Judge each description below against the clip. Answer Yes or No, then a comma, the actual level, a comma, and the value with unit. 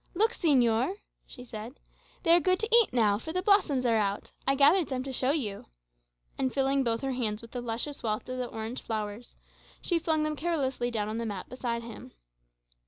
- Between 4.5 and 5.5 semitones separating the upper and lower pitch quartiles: Yes, average, 5.1 semitones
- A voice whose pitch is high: Yes, very high, 255 Hz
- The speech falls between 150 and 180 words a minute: No, fast, 205 wpm